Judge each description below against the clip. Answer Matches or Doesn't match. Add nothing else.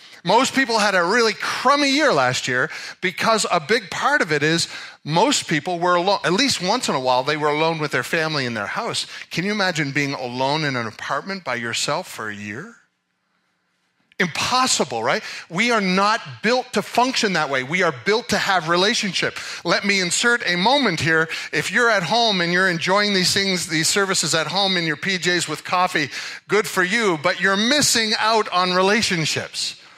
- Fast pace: Doesn't match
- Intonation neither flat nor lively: Doesn't match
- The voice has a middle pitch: Matches